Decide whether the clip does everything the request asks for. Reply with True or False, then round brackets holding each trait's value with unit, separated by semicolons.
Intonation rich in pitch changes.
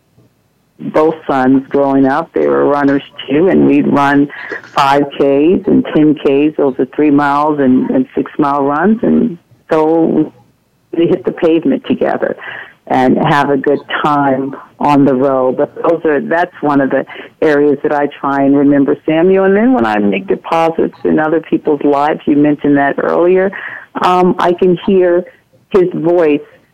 False (3.0 semitones)